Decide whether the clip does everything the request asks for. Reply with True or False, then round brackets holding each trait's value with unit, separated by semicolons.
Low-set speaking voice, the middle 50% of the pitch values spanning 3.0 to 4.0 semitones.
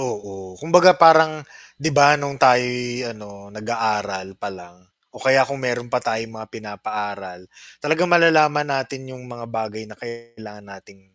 False (120 Hz; 5.1 semitones)